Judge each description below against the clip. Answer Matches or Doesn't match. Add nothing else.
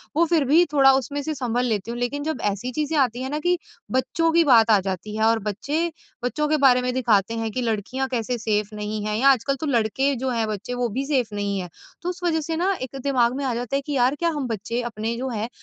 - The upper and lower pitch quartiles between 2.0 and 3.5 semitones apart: Doesn't match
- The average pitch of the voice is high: Matches